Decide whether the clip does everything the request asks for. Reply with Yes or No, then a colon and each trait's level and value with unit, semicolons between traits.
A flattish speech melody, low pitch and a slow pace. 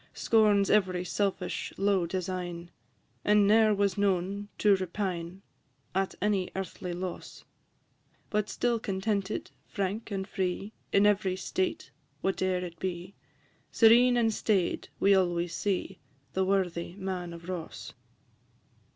No: narrow, 2.1 semitones; high, 190 Hz; slow, 120 wpm